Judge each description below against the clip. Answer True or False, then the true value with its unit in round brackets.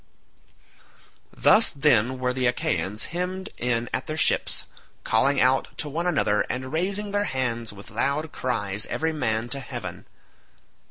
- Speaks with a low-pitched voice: True (130 Hz)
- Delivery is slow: False (145 wpm)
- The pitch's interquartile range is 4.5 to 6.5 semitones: True (5.4 semitones)